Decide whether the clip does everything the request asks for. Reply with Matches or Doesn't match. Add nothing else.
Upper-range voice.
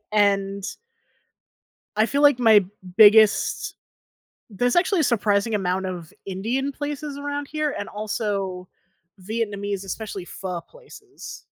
Matches